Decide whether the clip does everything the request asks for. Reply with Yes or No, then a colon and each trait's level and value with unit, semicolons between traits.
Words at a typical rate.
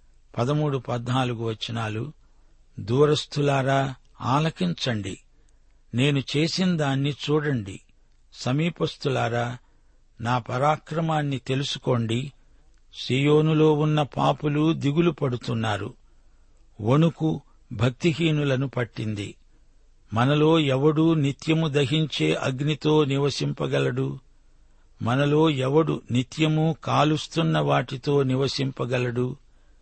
No: slow, 65 wpm